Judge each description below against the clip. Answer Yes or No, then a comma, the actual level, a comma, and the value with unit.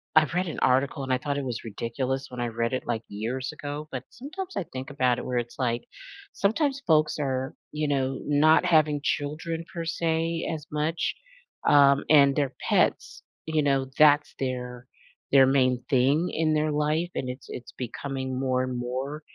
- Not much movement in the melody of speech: No, average, 3.3 semitones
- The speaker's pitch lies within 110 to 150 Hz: Yes, medium, 140 Hz